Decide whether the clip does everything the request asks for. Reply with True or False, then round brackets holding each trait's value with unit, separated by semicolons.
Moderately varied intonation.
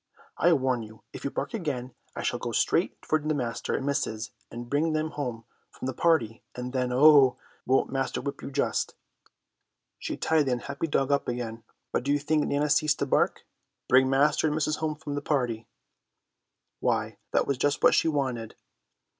True (3.3 semitones)